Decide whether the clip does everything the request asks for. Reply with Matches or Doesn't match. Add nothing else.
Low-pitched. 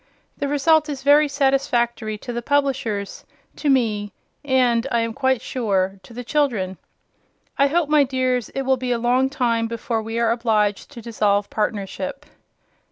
Doesn't match